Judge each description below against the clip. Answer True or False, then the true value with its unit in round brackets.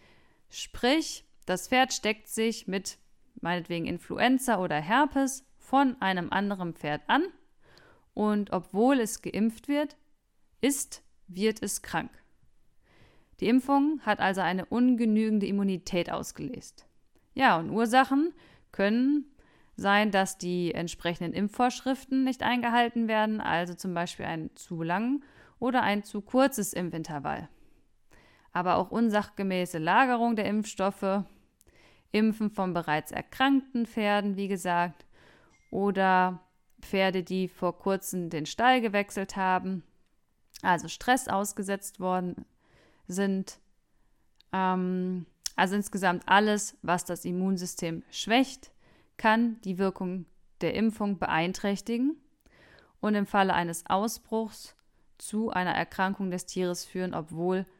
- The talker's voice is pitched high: True (200 Hz)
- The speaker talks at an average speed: False (110 wpm)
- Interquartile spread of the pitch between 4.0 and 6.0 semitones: True (4.3 semitones)